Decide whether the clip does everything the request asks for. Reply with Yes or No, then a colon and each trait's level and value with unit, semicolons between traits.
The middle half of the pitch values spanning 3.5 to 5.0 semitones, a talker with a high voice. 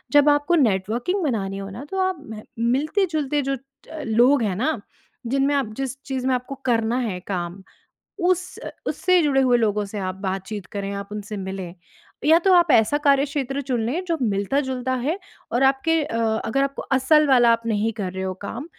No: wide, 5.4 semitones; very high, 255 Hz